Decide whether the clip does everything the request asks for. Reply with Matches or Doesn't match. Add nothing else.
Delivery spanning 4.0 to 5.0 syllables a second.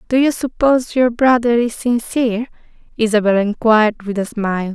Doesn't match